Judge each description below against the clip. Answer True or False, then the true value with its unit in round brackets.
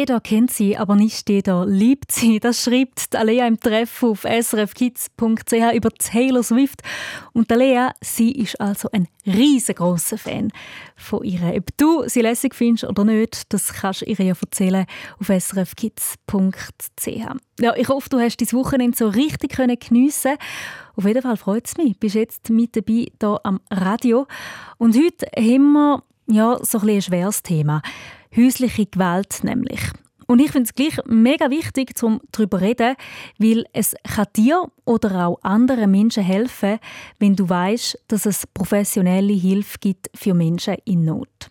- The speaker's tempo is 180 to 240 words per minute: False (160 wpm)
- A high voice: True (225 Hz)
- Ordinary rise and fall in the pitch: True (3.4 semitones)